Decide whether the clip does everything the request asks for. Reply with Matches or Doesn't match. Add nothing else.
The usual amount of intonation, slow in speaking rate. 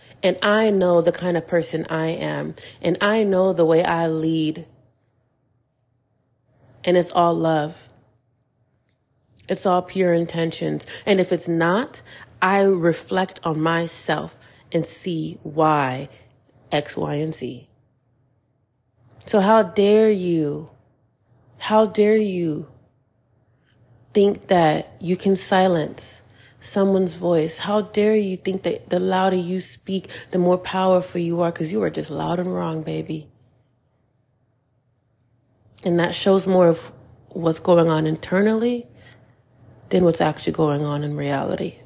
Doesn't match